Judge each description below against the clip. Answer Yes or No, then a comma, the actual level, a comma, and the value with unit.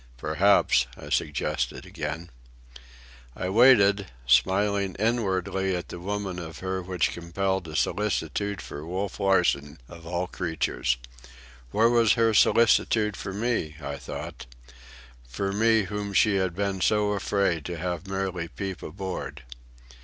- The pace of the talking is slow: Yes, slow, 125 wpm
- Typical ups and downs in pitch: Yes, average, 3.5 semitones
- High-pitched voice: No, very low, 95 Hz